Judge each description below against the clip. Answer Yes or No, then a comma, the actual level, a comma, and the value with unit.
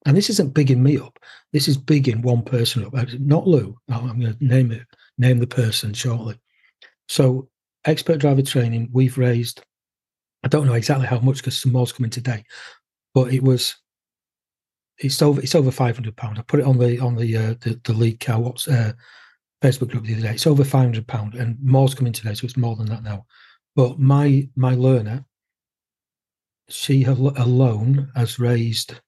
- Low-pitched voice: Yes, low, 125 Hz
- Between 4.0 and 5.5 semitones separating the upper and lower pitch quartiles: No, narrow, 2.4 semitones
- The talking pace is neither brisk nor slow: Yes, average, 190 wpm